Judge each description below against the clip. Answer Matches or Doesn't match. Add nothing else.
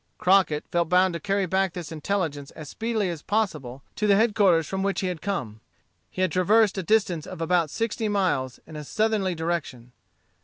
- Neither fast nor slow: Matches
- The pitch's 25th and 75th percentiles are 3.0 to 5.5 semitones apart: Matches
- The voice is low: Doesn't match